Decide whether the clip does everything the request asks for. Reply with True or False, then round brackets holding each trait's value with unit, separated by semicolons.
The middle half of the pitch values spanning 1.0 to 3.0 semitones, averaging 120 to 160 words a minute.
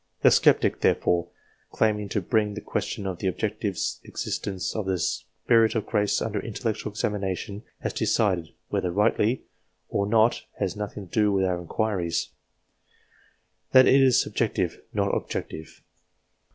True (2.5 semitones; 145 wpm)